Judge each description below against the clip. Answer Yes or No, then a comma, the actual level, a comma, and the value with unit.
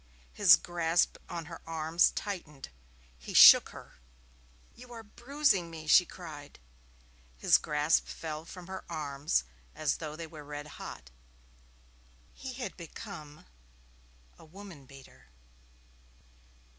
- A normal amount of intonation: Yes, average, 4.0 semitones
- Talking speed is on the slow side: Yes, slow, 120 wpm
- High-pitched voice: No, medium, 165 Hz